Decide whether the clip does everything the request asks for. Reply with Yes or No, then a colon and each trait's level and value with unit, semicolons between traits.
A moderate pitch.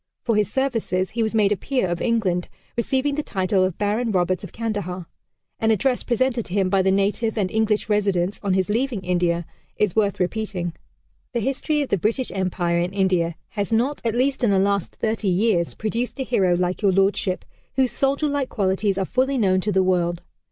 No: high, 205 Hz